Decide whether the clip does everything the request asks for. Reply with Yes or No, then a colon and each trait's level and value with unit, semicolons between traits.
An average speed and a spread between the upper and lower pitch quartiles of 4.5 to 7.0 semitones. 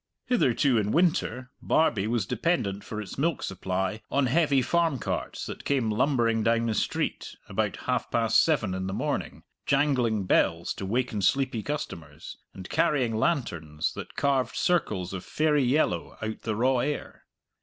Yes: average, 155 wpm; average, 5.1 semitones